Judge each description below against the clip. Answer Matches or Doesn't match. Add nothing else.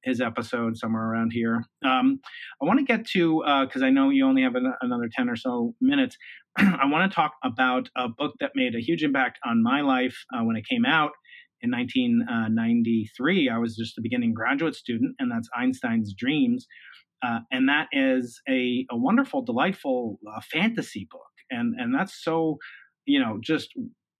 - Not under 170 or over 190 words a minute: Matches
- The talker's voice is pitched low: Doesn't match